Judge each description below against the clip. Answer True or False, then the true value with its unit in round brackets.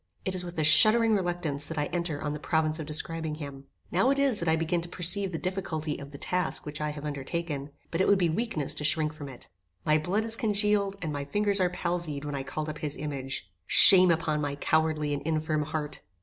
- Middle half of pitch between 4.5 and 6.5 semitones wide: False (3.4 semitones)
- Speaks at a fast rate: True (235 wpm)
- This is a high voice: False (160 Hz)